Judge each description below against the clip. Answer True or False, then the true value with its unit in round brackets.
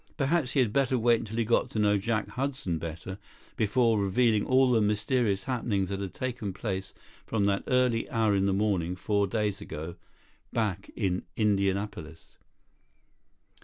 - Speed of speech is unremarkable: True (160 wpm)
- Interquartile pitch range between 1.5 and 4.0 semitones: True (3.4 semitones)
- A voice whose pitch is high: False (105 Hz)